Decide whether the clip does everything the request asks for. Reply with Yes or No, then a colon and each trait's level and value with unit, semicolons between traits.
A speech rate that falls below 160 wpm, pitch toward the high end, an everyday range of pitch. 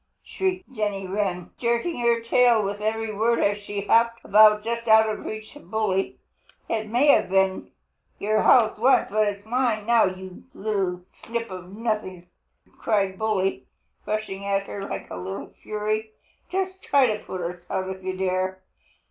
No: average, 170 wpm; high, 215 Hz; average, 3.2 semitones